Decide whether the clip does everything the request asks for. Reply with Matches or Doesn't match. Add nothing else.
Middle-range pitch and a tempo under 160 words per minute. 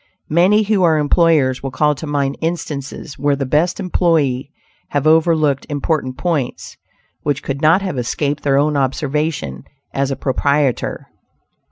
Matches